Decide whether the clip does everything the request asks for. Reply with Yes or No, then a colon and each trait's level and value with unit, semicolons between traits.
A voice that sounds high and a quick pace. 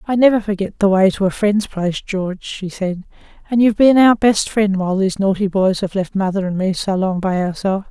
Yes: high, 195 Hz; fast, 235 wpm